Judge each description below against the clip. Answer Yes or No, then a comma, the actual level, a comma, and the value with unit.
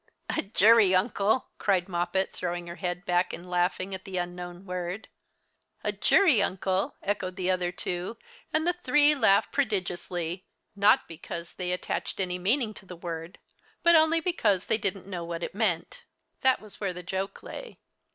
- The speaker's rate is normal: Yes, average, 170 wpm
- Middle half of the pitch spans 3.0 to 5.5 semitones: Yes, average, 3.3 semitones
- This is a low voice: No, medium, 185 Hz